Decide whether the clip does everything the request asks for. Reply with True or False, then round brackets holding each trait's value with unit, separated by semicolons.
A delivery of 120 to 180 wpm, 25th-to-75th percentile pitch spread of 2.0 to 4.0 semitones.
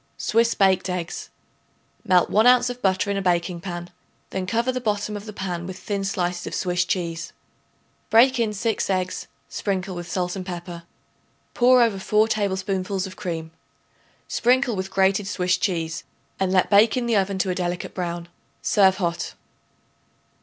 True (165 wpm; 2.9 semitones)